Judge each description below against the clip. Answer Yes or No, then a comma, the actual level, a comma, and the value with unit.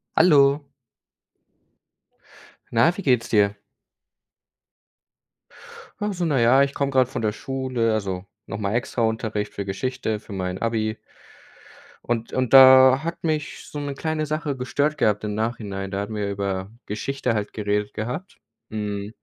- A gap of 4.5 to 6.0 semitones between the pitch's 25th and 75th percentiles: Yes, average, 4.8 semitones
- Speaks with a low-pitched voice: Yes, low, 115 Hz